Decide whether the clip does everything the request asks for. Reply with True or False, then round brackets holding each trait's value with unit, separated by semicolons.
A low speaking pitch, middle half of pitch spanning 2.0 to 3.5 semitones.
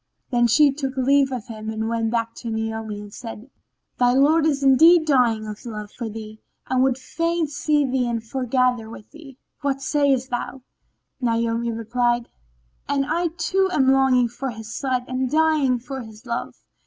False (250 Hz; 3.2 semitones)